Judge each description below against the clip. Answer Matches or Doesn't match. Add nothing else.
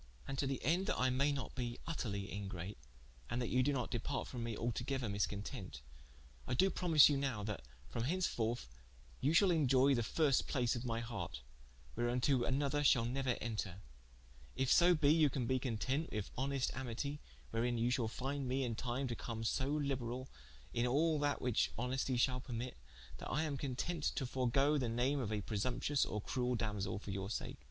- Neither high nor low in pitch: Doesn't match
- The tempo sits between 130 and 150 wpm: Doesn't match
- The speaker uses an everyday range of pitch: Matches